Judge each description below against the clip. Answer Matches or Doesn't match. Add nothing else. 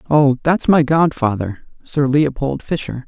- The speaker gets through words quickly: Doesn't match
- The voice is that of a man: Matches